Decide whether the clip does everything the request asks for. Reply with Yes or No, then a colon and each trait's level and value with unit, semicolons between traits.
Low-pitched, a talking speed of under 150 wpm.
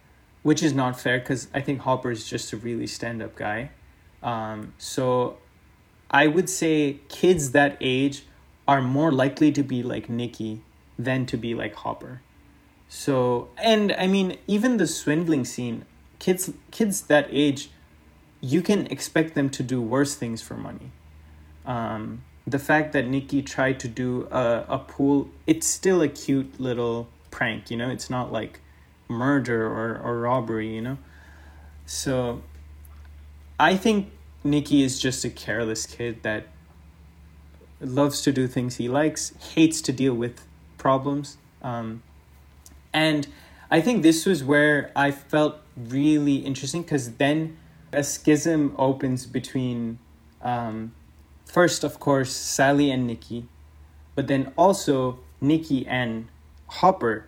Yes: low, 130 Hz; average, 140 wpm